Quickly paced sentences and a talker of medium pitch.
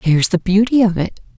No: fast, 215 wpm; high, 195 Hz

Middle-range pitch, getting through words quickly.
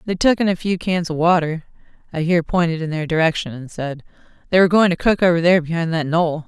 Yes: medium, 170 Hz; fast, 240 wpm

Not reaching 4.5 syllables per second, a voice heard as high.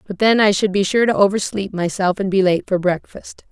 No: 5.5 syllables/s; high, 195 Hz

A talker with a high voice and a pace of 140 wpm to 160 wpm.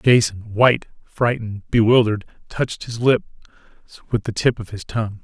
No: low, 110 Hz; average, 150 wpm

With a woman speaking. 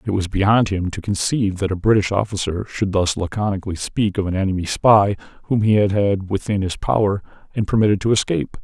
No: male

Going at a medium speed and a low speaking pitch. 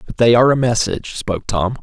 No: fast, 230 wpm; low, 115 Hz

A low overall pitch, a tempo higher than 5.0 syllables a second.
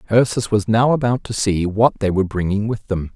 Yes: low, 110 Hz; 5.5 syllables/s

